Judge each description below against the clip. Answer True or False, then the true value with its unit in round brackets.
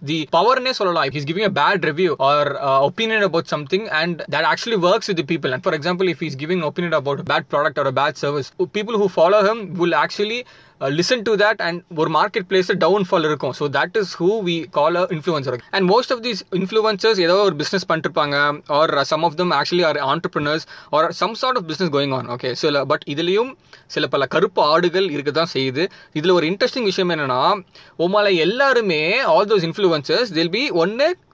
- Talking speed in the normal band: False (205 wpm)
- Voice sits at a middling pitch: True (175 Hz)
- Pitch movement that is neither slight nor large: True (4.7 semitones)